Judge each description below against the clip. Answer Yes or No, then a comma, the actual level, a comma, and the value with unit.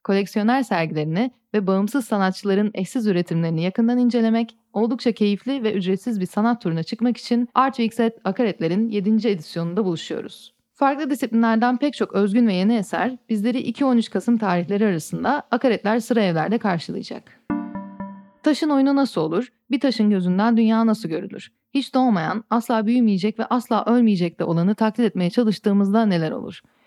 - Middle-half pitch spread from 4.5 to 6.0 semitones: No, average, 3.6 semitones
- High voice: Yes, high, 220 Hz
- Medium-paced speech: No, fast, 145 wpm